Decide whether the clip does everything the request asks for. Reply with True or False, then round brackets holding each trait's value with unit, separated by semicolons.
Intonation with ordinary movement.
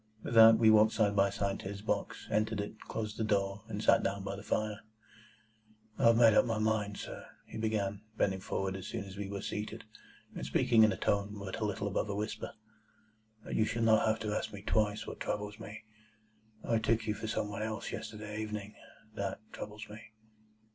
False (1.5 semitones)